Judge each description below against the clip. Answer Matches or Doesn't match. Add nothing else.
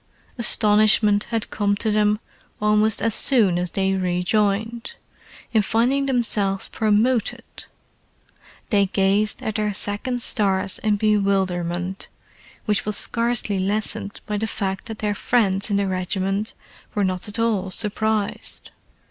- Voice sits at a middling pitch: Doesn't match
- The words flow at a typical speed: Doesn't match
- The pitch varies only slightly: Matches